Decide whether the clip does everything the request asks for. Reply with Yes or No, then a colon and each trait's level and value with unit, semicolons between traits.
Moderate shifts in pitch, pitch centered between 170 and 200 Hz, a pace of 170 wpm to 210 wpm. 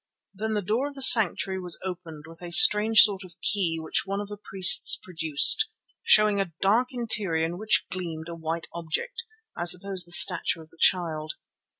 Yes: average, 4.0 semitones; medium, 185 Hz; average, 190 wpm